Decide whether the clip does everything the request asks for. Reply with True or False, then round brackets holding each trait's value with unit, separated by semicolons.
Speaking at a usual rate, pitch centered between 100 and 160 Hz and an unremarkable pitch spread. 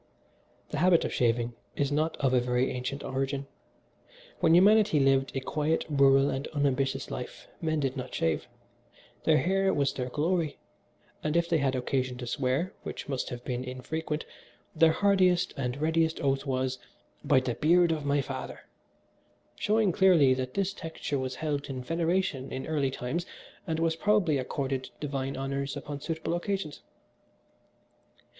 True (155 wpm; 140 Hz; 3.7 semitones)